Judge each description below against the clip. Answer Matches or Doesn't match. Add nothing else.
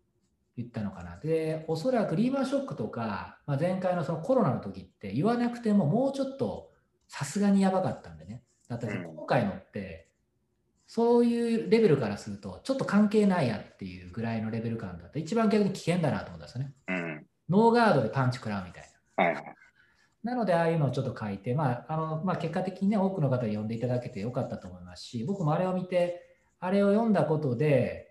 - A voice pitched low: Doesn't match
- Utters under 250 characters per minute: Doesn't match